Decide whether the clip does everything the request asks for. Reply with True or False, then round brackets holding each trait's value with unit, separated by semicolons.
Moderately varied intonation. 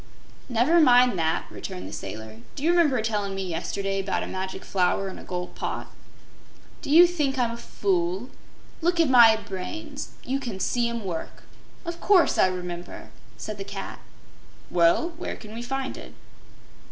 False (6.4 semitones)